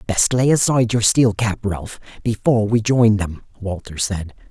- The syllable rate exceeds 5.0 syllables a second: No, 4.7 syllables/s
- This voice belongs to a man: Yes, male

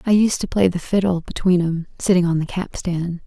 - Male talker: No, female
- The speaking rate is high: Yes, fast, 220 wpm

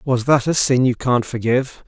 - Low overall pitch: Yes, low, 125 Hz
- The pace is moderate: No, fast, 225 wpm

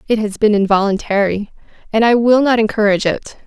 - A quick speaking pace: No, average, 175 wpm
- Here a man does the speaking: No, female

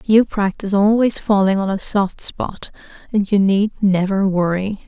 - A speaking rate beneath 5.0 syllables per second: Yes, 4.5 syllables/s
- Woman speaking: Yes, female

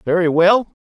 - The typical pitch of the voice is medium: Yes, medium, 180 Hz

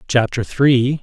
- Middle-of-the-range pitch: No, low, 125 Hz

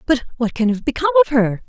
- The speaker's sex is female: Yes, female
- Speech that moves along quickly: Yes, fast, 250 wpm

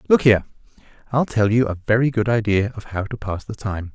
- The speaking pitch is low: Yes, low, 110 Hz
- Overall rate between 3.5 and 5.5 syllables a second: No, 5.9 syllables/s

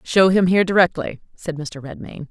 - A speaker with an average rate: Yes, average, 180 wpm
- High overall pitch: No, medium, 170 Hz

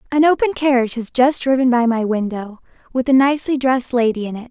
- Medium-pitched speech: No, very high, 250 Hz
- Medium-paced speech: No, fast, 215 wpm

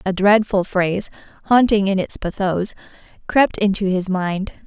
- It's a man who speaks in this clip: No, female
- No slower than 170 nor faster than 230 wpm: No, average, 140 wpm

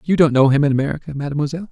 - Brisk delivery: Yes, fast, 245 wpm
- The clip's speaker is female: No, male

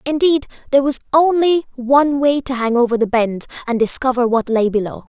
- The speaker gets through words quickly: No, average, 185 wpm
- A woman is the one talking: Yes, female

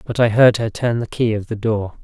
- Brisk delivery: Yes, fast, 295 wpm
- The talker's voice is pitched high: No, low, 110 Hz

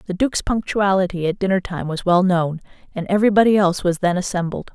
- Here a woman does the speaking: Yes, female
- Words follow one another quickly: No, average, 190 wpm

